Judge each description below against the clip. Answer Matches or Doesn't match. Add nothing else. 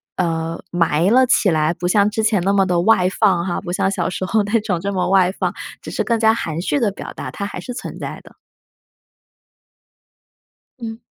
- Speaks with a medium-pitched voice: Doesn't match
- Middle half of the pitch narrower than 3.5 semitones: Doesn't match